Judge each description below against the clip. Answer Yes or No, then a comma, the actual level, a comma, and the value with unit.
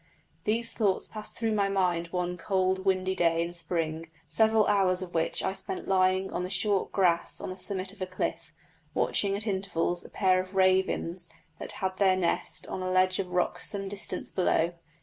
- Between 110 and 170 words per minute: No, average, 190 wpm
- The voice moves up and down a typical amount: No, narrow, 1.5 semitones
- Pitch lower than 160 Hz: No, medium, 185 Hz